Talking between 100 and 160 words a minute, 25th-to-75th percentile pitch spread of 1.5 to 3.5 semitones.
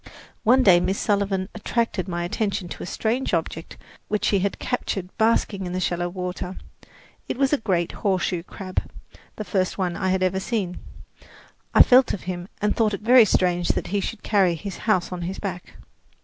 No: average, 190 wpm; average, 3.0 semitones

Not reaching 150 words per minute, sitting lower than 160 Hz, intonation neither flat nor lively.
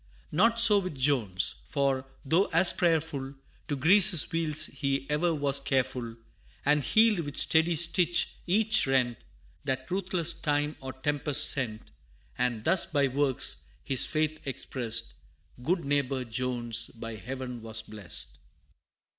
Yes: slow, 135 wpm; medium, 140 Hz; average, 4.5 semitones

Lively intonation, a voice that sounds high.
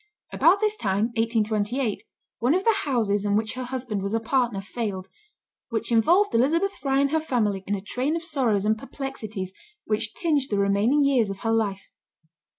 No: average, 5.0 semitones; high, 230 Hz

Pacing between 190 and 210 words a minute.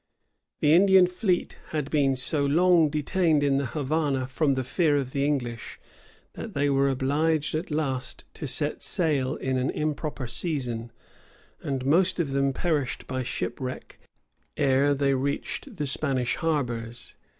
No: average, 150 wpm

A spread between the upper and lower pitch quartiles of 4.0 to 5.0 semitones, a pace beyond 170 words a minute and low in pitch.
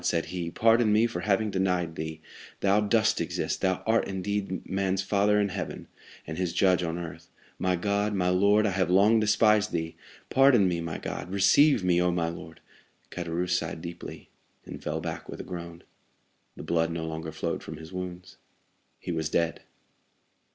No: average, 3.3 semitones; average, 180 wpm; very low, 90 Hz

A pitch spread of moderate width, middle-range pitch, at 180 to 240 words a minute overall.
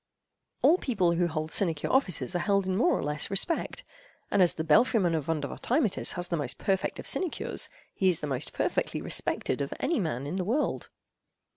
Yes: average, 4.2 semitones; medium, 180 Hz; average, 190 wpm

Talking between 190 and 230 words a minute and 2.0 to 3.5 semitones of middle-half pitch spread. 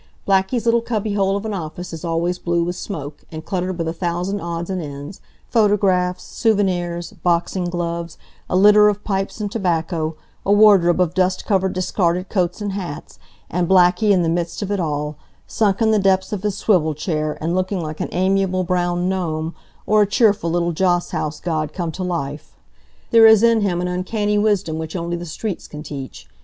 Yes: average, 195 wpm; average, 2.9 semitones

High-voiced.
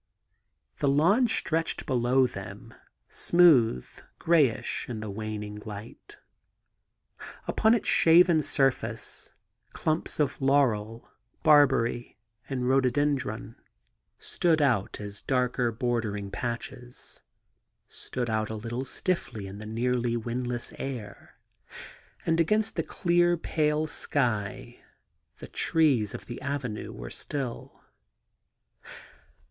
No: low, 125 Hz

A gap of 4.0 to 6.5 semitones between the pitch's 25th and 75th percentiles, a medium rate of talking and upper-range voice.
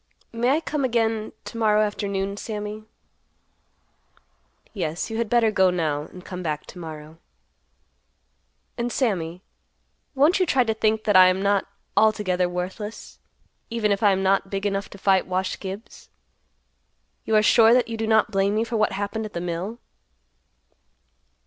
No: average, 3.1 semitones; average, 160 wpm; high, 205 Hz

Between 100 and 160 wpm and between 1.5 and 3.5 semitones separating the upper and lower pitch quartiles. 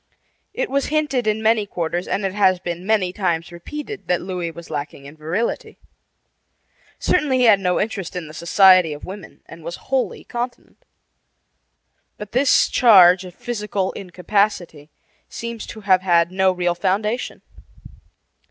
No: average, 150 wpm; average, 4.1 semitones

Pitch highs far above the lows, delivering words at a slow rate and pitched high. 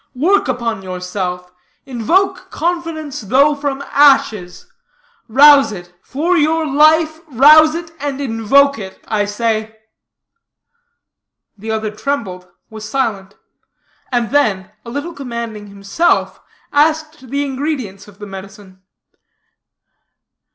Yes: wide, 6.2 semitones; slow, 110 wpm; very high, 255 Hz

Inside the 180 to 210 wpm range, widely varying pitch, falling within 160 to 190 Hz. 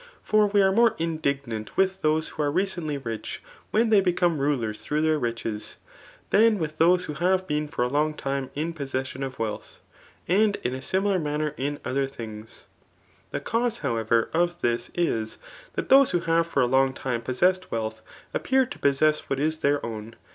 No: average, 185 wpm; wide, 5.7 semitones; medium, 150 Hz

